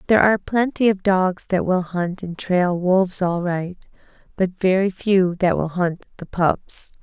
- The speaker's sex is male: No, female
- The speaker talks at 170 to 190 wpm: Yes, average, 180 wpm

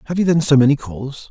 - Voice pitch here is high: No, medium, 140 Hz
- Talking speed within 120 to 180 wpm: No, fast, 275 wpm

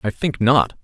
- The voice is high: No, low, 115 Hz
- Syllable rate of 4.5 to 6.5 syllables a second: No, 4.2 syllables/s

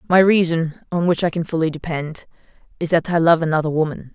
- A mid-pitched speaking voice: Yes, medium, 165 Hz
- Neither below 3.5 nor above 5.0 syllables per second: No, 5.9 syllables/s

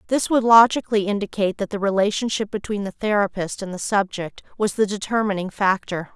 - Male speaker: No, female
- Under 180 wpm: Yes, average, 165 wpm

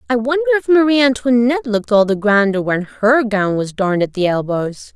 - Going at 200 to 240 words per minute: Yes, fast, 205 wpm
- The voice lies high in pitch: Yes, high, 230 Hz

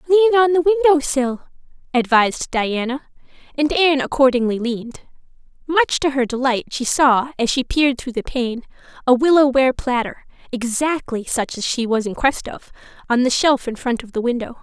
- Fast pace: No, average, 175 wpm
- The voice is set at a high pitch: Yes, very high, 265 Hz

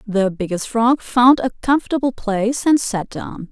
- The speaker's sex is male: No, female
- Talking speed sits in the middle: Yes, average, 170 wpm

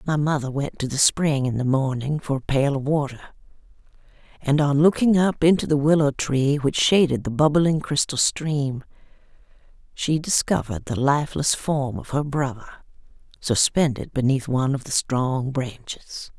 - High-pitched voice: No, medium, 140 Hz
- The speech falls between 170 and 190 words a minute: No, average, 155 wpm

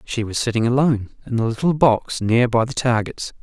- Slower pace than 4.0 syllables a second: No, 5.5 syllables/s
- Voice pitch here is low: Yes, low, 120 Hz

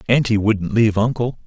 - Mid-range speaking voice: No, low, 110 Hz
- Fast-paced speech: No, average, 165 wpm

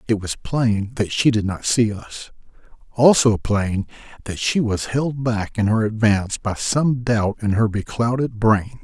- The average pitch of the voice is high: No, low, 110 Hz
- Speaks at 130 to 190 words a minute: Yes, average, 175 wpm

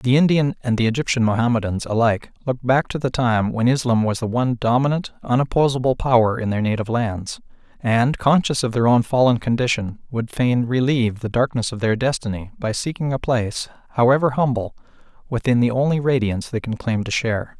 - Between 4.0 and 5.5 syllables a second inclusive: No, 5.8 syllables/s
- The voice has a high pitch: No, low, 120 Hz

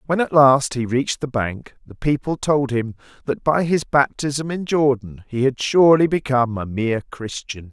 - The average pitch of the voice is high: No, low, 135 Hz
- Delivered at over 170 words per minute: Yes, average, 185 wpm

